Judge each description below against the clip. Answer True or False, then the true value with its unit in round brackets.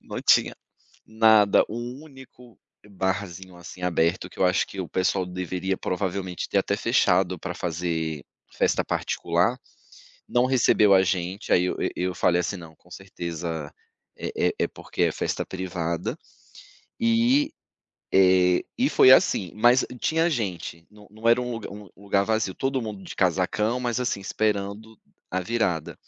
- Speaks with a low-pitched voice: True (95 Hz)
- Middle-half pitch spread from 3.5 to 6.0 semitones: True (4.0 semitones)